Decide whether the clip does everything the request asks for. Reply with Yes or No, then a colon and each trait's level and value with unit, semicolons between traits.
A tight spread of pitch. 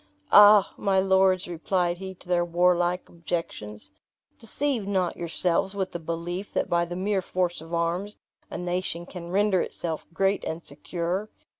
Yes: narrow, 2.0 semitones